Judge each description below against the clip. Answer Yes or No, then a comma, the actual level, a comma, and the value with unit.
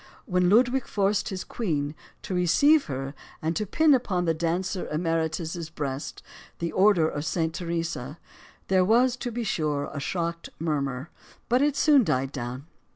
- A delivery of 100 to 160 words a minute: Yes, average, 155 wpm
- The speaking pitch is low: No, medium, 170 Hz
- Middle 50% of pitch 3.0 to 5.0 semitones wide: No, wide, 5.4 semitones